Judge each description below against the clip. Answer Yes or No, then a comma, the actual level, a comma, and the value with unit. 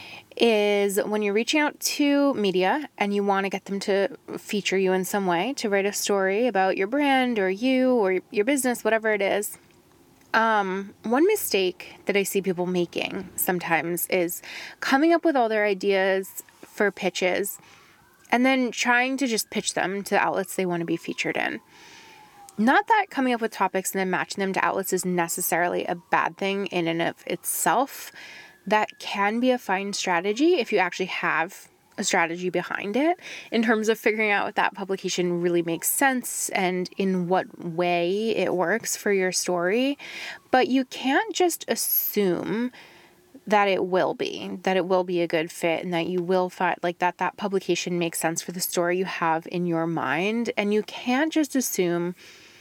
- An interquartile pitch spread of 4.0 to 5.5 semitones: Yes, average, 4.5 semitones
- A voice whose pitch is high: Yes, high, 195 Hz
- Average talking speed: Yes, average, 185 wpm